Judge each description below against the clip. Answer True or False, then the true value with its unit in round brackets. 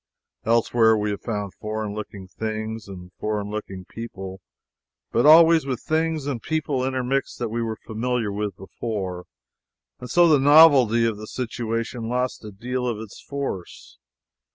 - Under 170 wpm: True (155 wpm)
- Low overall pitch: True (115 Hz)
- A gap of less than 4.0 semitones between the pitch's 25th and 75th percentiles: True (3.5 semitones)